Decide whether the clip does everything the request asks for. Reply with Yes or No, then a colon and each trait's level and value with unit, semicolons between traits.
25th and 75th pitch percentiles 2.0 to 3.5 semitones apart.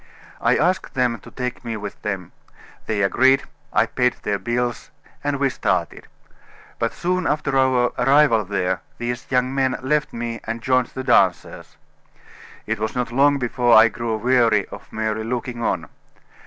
Yes: average, 2.9 semitones